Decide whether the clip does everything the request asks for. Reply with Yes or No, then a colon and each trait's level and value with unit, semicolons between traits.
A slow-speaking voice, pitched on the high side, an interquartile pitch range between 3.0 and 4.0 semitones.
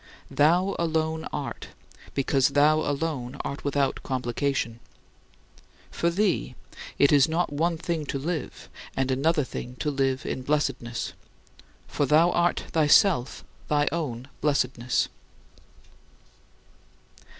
No: slow, 110 wpm; medium, 145 Hz; average, 3.4 semitones